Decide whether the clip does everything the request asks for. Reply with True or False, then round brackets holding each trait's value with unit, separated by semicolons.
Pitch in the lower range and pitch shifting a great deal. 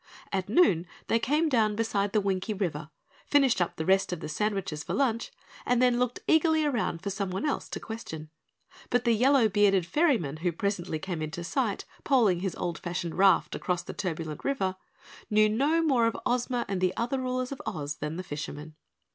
False (200 Hz; 6.0 semitones)